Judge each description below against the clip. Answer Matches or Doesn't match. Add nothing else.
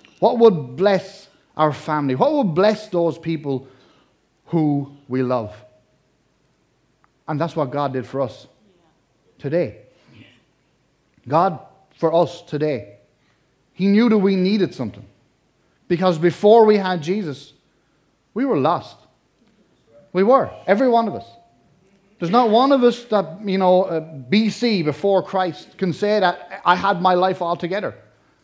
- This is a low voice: Doesn't match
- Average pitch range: Doesn't match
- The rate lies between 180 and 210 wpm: Doesn't match